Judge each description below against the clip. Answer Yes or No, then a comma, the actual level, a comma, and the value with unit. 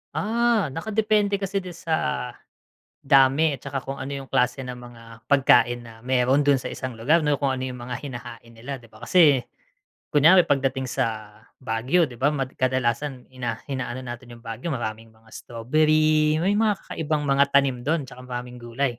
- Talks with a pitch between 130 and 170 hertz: Yes, low, 135 Hz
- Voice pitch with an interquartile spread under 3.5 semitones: No, average, 4.1 semitones